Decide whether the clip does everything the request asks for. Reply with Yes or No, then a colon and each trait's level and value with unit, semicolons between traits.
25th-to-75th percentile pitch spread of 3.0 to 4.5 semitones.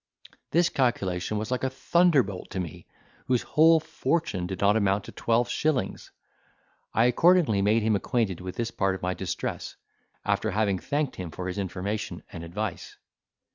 No: wide, 5.4 semitones